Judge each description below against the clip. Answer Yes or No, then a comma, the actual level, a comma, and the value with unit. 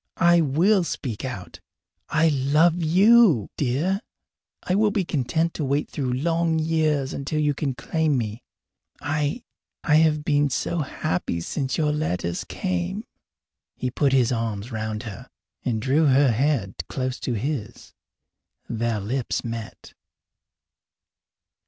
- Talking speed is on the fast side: No, slow, 135 wpm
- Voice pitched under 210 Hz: Yes, medium, 140 Hz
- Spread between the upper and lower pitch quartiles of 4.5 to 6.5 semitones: Yes, average, 5.1 semitones